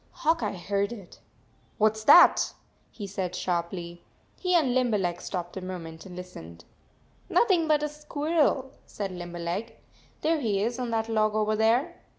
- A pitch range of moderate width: No, wide, 6.4 semitones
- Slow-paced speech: No, average, 170 wpm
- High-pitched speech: Yes, high, 215 Hz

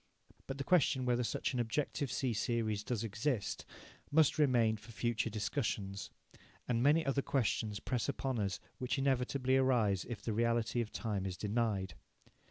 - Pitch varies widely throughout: No, average, 3.6 semitones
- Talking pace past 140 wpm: Yes, average, 160 wpm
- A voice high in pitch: No, low, 120 Hz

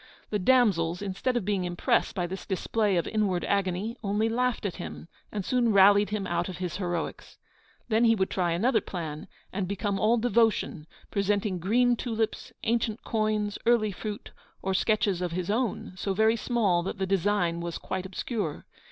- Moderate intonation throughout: Yes, average, 3.4 semitones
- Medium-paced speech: Yes, average, 175 wpm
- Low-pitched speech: No, high, 200 Hz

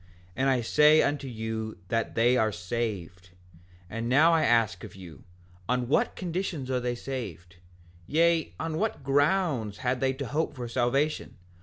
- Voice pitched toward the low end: Yes, low, 125 Hz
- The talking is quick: No, average, 160 wpm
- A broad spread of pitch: No, average, 4.8 semitones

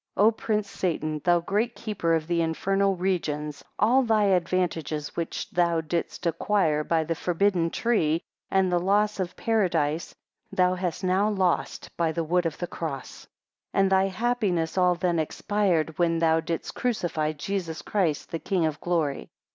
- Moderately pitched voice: Yes, medium, 175 Hz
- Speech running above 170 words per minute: No, average, 165 wpm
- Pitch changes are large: No, average, 3.3 semitones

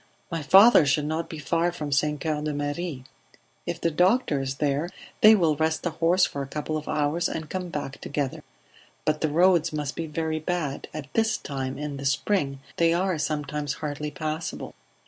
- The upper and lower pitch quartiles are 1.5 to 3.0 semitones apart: Yes, narrow, 2.6 semitones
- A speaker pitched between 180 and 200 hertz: No, medium, 155 Hz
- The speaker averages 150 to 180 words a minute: No, average, 190 wpm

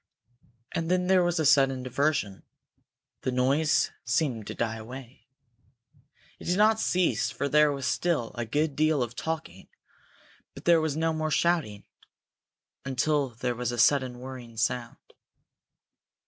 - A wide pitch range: No, average, 4.6 semitones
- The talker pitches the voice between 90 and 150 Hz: Yes, medium, 140 Hz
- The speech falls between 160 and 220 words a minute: No, average, 145 wpm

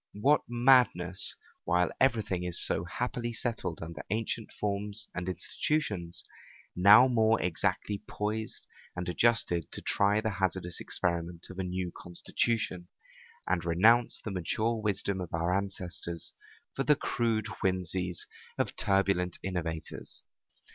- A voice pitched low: Yes, very low, 95 Hz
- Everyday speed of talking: No, slow, 125 wpm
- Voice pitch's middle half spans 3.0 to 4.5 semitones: Yes, average, 3.9 semitones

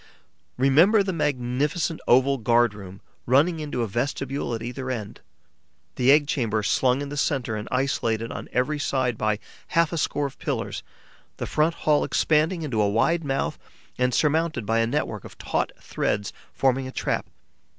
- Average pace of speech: Yes, average, 170 wpm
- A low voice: Yes, low, 130 Hz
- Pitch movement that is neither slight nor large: Yes, average, 4.3 semitones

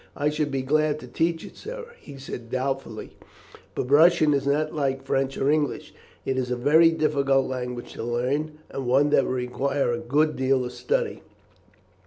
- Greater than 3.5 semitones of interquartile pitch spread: No, average, 3.0 semitones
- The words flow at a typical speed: Yes, average, 185 wpm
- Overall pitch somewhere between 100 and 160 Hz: Yes, low, 135 Hz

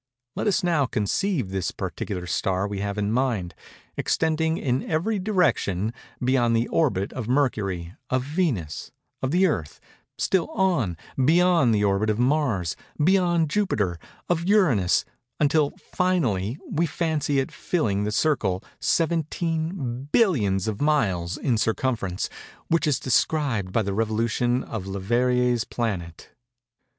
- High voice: No, low, 125 Hz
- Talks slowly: Yes, slow, 115 wpm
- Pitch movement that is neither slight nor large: No, wide, 7.9 semitones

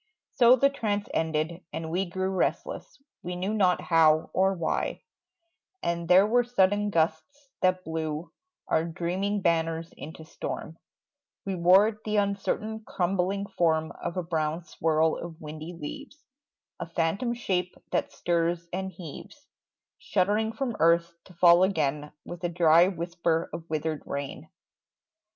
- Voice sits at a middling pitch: Yes, medium, 175 Hz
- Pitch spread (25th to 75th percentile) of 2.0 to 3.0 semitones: No, average, 3.4 semitones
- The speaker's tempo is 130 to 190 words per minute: Yes, average, 140 wpm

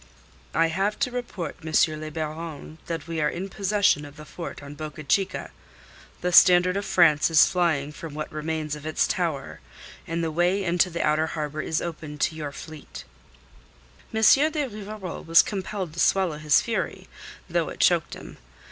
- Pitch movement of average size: Yes, average, 3.3 semitones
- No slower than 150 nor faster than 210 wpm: Yes, average, 175 wpm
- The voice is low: No, medium, 165 Hz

